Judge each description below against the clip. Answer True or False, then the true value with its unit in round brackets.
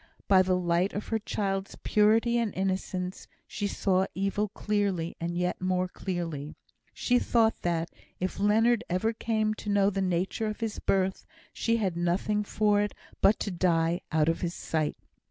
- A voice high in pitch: True (195 Hz)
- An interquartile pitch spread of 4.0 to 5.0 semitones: False (3.0 semitones)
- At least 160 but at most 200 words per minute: True (170 wpm)